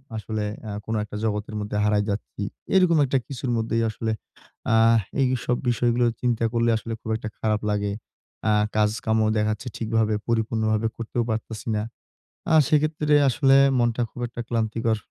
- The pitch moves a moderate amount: No, narrow, 1.8 semitones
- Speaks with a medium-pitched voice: No, low, 115 Hz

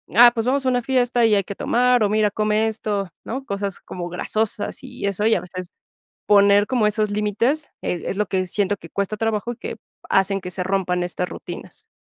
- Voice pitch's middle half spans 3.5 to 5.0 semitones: No, average, 2.9 semitones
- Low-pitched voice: No, high, 210 Hz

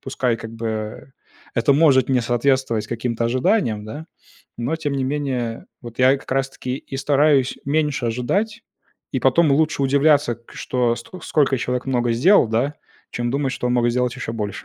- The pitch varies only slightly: No, average, 3.2 semitones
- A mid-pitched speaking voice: No, low, 130 Hz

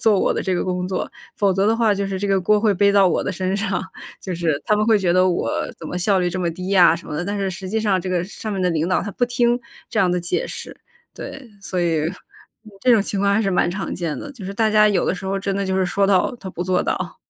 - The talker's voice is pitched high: Yes, high, 195 Hz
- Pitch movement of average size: No, narrow, 2.3 semitones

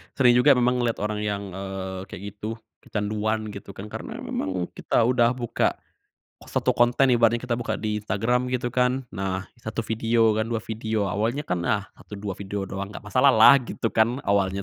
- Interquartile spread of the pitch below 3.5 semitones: Yes, average, 3.1 semitones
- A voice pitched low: Yes, low, 110 Hz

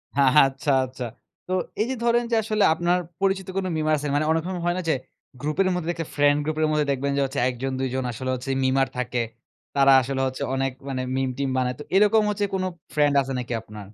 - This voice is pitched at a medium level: Yes, medium, 145 Hz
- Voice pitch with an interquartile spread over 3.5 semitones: Yes, average, 4.7 semitones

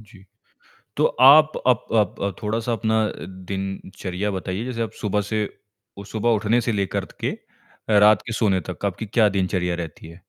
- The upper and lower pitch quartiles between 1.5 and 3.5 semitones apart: Yes, narrow, 2.6 semitones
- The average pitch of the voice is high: No, low, 105 Hz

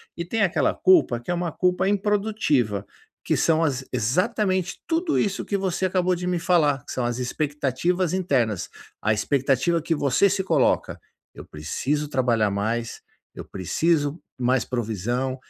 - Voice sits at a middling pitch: Yes, medium, 150 Hz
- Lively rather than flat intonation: Yes, wide, 6.8 semitones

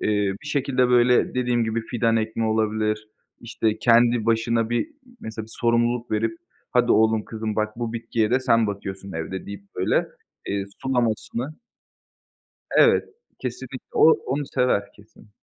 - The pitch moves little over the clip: Yes, narrow, 2.1 semitones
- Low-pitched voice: Yes, low, 115 Hz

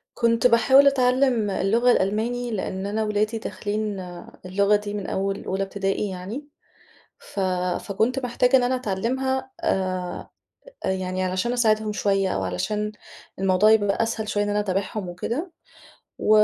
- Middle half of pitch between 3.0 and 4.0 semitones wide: Yes, average, 3.6 semitones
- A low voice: No, high, 210 Hz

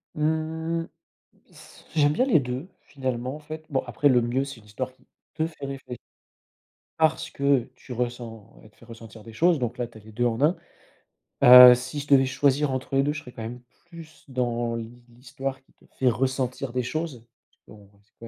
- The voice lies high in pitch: No, low, 130 Hz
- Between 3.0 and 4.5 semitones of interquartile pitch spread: Yes, average, 3.4 semitones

